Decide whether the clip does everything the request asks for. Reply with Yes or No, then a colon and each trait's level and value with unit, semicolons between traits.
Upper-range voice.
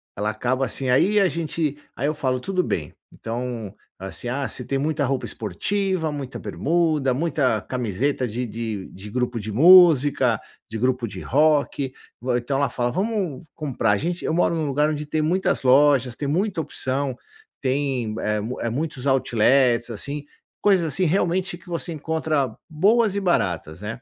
No: low, 135 Hz